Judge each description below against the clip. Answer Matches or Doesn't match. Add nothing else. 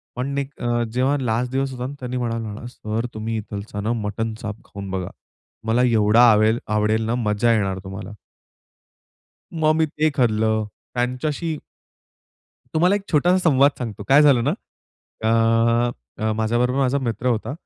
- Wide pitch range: Doesn't match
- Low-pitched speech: Matches